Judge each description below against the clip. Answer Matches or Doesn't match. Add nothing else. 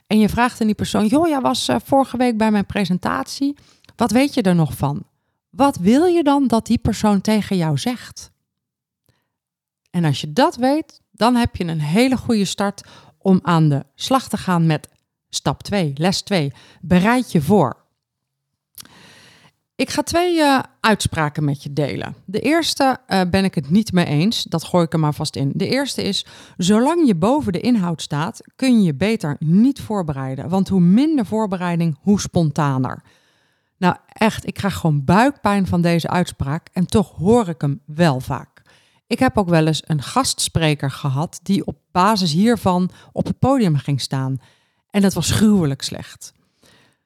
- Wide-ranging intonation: Matches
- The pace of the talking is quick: Doesn't match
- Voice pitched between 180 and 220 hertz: Matches